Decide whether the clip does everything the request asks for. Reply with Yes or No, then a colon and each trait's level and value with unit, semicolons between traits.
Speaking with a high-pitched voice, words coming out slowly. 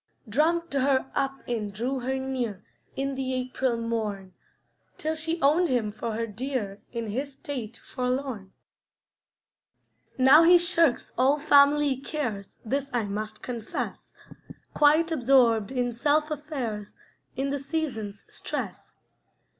Yes: very high, 260 Hz; slow, 125 wpm